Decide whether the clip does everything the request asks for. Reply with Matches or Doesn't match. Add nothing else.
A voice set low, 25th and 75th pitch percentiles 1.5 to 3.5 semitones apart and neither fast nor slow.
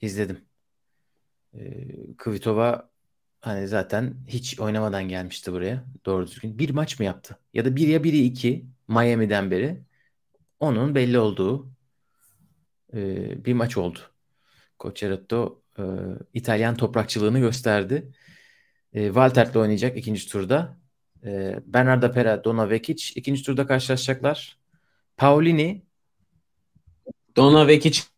Doesn't match